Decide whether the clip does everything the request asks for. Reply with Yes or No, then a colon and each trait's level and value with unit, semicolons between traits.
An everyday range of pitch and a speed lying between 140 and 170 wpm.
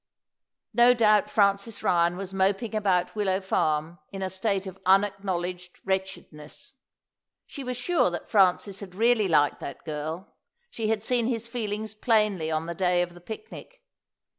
Yes: average, 3.4 semitones; average, 155 wpm